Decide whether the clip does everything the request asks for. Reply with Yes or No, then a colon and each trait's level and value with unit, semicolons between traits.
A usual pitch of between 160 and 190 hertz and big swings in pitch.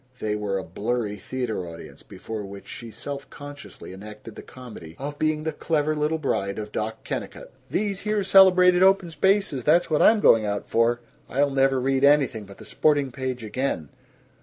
No: low, 130 Hz; wide, 6.3 semitones